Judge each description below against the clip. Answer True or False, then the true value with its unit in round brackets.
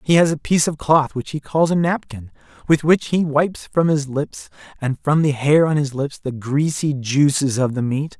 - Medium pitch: True (145 Hz)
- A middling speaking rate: False (225 wpm)